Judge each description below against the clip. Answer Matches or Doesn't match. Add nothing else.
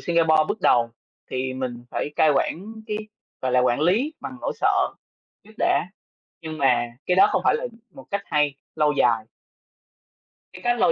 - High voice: Doesn't match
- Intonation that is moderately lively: Doesn't match